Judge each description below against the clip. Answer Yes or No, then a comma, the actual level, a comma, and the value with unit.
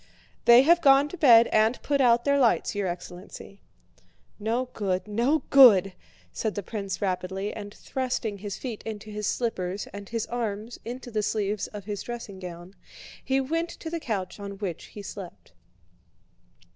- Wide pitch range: No, average, 3.7 semitones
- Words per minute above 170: No, average, 165 wpm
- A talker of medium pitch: No, high, 215 Hz